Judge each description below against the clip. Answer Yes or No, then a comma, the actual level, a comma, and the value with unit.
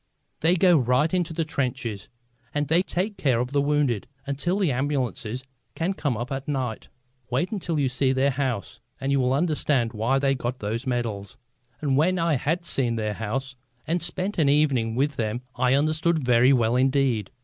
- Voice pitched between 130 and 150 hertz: Yes, low, 135 Hz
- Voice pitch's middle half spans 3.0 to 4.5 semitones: Yes, average, 4.0 semitones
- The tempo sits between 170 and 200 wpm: Yes, average, 185 wpm